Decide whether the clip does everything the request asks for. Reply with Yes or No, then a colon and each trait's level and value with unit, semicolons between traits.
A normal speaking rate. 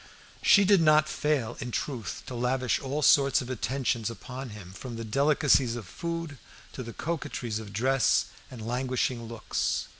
Yes: average, 160 wpm